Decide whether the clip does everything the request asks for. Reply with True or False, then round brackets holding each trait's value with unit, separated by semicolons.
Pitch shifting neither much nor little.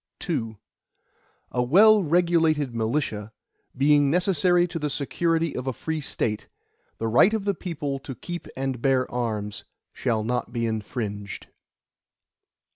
False (6.2 semitones)